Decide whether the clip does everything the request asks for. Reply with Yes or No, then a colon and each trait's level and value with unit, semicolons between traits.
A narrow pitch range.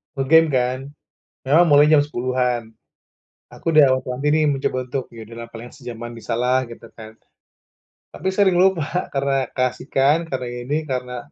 No: average, 3.3 semitones